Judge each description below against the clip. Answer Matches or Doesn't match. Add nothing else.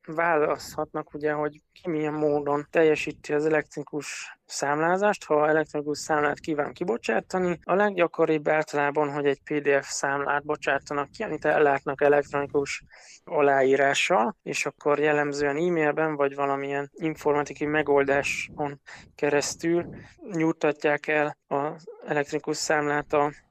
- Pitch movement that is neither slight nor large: Doesn't match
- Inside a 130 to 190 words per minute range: Doesn't match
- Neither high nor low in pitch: Matches